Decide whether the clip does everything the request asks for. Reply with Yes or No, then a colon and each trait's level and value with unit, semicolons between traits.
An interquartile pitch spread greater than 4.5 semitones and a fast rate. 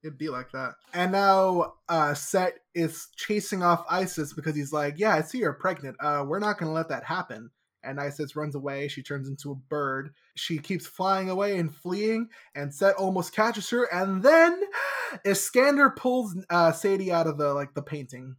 No: average, 5.1 semitones; average, 195 wpm